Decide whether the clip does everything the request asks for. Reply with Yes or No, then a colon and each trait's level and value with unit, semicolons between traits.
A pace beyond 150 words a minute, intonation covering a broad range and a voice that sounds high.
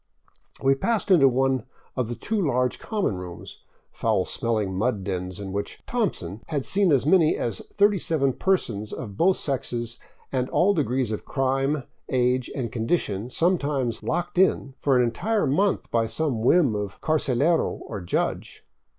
No: average, 160 wpm; wide, 6.3 semitones; low, 130 Hz